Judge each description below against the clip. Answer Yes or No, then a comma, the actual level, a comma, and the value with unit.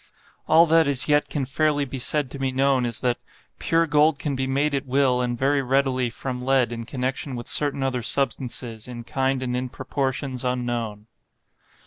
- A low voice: Yes, low, 130 Hz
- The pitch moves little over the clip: Yes, narrow, 2.0 semitones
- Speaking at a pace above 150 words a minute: Yes, average, 185 wpm